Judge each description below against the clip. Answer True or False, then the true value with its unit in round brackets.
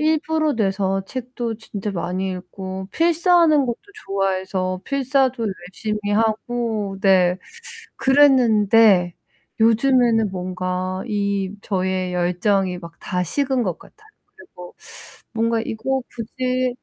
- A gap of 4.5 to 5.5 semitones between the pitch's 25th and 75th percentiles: True (5.1 semitones)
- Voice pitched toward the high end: True (210 Hz)